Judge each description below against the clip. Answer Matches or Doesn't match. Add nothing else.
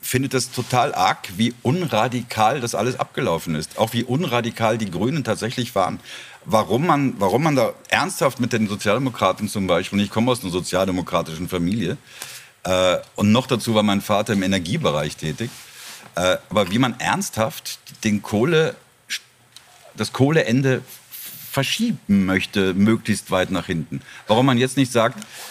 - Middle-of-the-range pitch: Doesn't match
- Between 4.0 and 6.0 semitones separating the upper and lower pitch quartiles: Matches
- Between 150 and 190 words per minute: Matches